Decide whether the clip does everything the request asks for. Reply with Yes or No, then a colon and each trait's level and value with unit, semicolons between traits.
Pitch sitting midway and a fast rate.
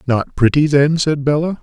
No: medium, 145 Hz; average, 185 wpm